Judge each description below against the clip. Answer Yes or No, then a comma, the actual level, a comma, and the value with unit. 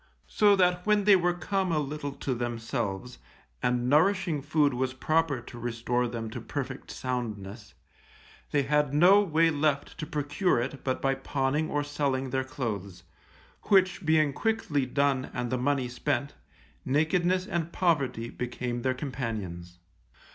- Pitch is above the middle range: No, medium, 140 Hz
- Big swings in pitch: No, average, 4.4 semitones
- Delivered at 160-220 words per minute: No, average, 145 wpm